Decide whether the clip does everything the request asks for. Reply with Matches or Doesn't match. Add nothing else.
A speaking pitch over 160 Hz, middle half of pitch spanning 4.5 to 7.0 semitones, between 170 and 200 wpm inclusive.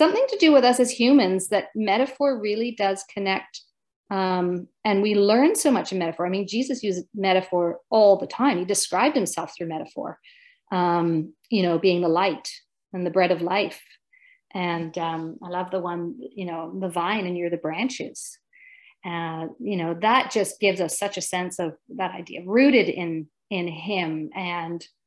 Matches